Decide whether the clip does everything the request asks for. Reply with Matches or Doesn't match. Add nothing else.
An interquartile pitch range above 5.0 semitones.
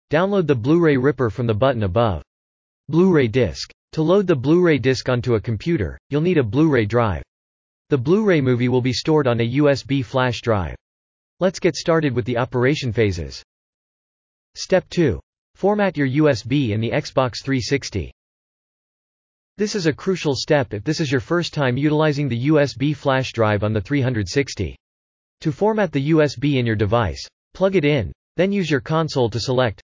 Matches